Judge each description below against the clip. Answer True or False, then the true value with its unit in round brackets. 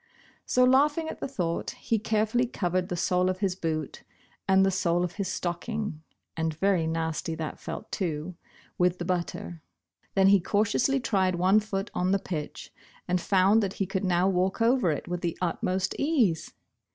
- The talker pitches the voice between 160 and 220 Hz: True (185 Hz)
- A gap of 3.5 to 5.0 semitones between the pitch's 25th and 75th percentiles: False (3.1 semitones)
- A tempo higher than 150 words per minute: True (175 wpm)